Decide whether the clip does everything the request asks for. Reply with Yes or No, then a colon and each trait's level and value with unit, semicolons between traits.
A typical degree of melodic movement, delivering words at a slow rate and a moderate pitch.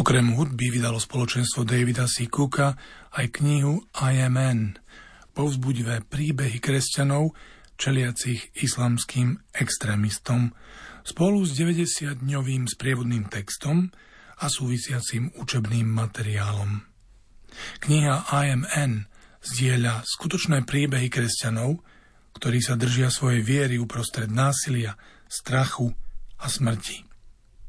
No: average, 3.2 semitones; slow, 95 wpm; low, 125 Hz